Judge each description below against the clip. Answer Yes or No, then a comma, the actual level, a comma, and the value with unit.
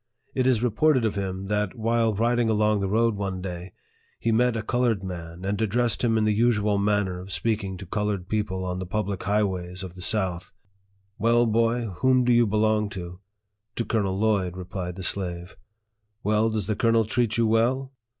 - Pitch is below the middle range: Yes, low, 105 Hz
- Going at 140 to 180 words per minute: No, average, 200 wpm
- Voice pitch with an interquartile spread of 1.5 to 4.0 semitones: Yes, average, 3.2 semitones